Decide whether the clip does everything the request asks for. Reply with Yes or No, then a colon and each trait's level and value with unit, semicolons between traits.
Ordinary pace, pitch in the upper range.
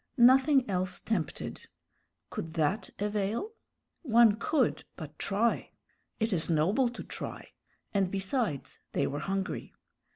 No: slow, 120 wpm; high, 205 Hz